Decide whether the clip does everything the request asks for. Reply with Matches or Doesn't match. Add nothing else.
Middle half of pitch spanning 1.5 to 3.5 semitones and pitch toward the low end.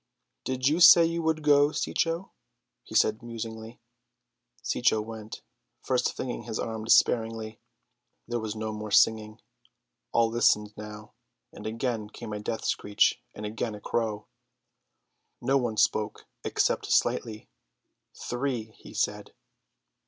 Matches